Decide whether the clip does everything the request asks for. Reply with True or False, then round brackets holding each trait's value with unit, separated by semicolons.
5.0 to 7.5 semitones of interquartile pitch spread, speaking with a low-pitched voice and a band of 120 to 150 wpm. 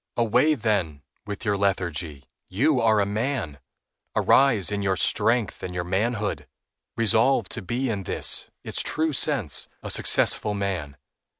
False (4.3 semitones; 105 Hz; 140 wpm)